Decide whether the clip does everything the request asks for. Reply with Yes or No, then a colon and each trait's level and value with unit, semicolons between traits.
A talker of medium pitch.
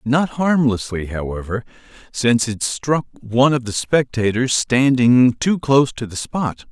No: low, 125 Hz